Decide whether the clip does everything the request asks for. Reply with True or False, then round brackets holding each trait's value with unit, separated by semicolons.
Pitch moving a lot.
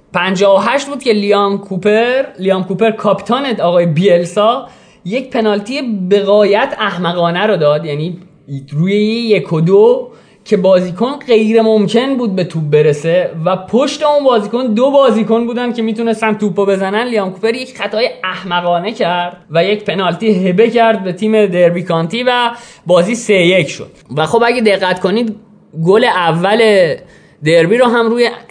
False (4.3 semitones)